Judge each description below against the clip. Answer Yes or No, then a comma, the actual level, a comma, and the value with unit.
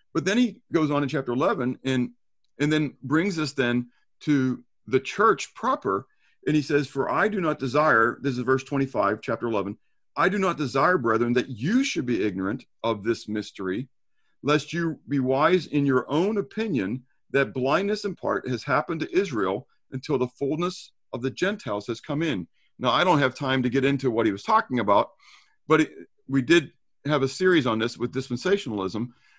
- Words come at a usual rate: Yes, average, 190 wpm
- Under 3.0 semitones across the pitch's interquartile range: No, average, 4.4 semitones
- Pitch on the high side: No, low, 135 Hz